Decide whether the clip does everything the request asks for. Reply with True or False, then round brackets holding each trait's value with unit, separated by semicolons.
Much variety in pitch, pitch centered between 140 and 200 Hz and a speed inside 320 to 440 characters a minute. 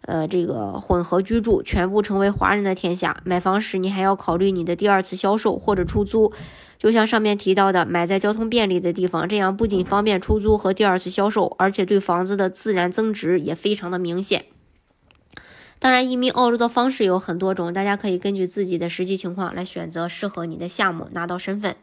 False (2.5 semitones; 190 Hz; 330 characters per minute)